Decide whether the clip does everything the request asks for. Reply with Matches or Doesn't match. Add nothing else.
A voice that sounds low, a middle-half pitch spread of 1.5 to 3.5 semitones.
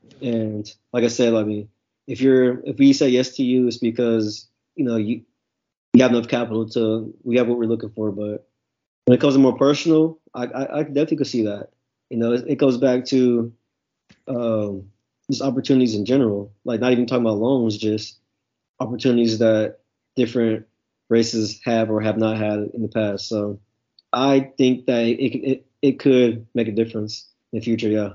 Matches